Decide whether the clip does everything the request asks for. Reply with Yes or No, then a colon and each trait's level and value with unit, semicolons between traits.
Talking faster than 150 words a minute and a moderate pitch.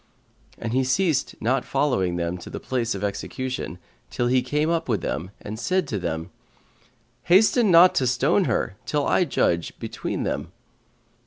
No: average, 165 wpm; low, 130 Hz